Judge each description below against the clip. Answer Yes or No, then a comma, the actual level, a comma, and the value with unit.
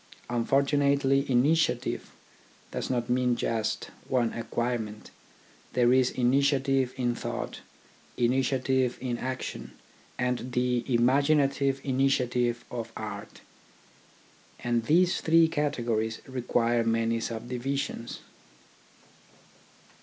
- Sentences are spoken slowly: Yes, slow, 95 wpm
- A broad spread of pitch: No, narrow, 2.4 semitones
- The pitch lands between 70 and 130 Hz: Yes, low, 125 Hz